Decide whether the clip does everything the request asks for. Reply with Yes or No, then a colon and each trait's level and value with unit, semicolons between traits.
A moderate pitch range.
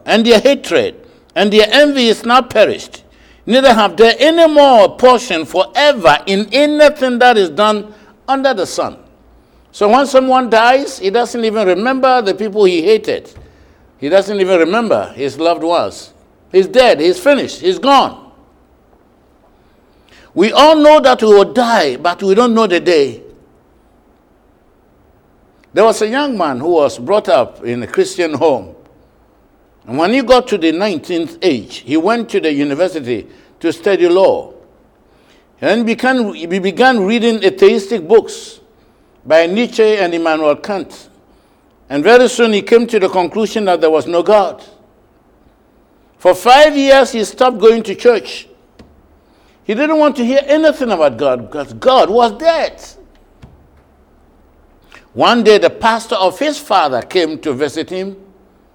No: wide, 6.4 semitones